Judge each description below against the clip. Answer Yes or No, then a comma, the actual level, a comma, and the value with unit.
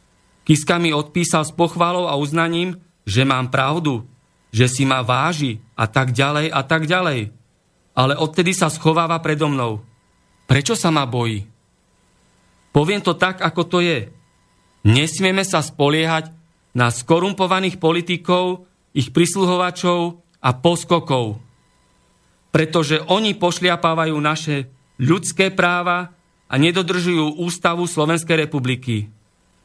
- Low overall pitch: No, medium, 160 Hz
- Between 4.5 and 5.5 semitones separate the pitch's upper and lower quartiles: Yes, average, 5.2 semitones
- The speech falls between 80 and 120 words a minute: Yes, average, 115 wpm